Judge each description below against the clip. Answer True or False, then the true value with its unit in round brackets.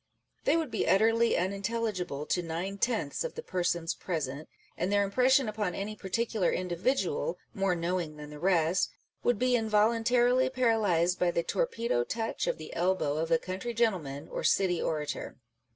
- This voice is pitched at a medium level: False (195 Hz)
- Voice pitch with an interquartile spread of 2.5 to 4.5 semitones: False (5.2 semitones)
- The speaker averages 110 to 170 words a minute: True (165 wpm)